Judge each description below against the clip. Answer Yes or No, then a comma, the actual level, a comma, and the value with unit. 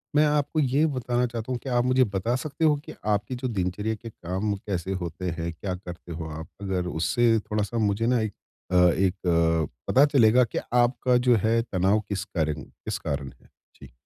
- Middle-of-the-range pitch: No, low, 105 Hz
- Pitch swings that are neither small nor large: No, wide, 5.7 semitones